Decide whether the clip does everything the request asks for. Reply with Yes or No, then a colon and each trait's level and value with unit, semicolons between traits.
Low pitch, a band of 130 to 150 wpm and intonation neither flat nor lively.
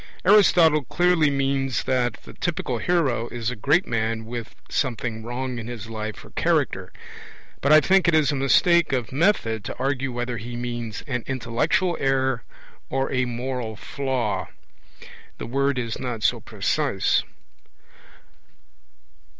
Yes: low, 130 Hz; average, 140 wpm; average, 3.3 semitones